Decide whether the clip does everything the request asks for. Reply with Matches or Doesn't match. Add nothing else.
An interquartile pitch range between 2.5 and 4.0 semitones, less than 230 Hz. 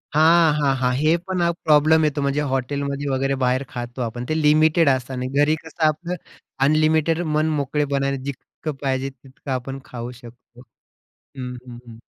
Matches